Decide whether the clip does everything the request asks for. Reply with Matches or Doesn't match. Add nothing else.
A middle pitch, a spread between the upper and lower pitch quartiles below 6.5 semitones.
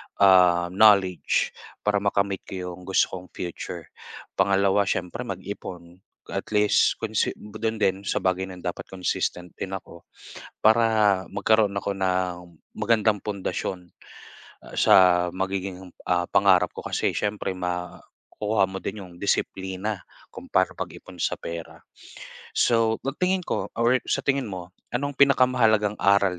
Doesn't match